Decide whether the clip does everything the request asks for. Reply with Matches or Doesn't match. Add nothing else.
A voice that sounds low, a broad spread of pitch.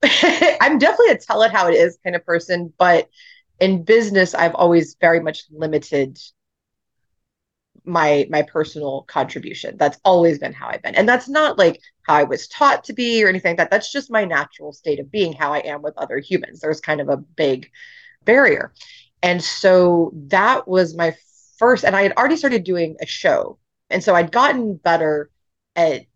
Doesn't match